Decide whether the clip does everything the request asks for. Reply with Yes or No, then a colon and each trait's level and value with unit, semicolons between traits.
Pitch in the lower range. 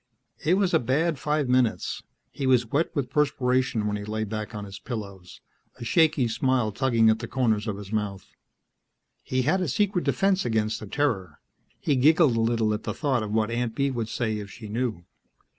Yes: low, 120 Hz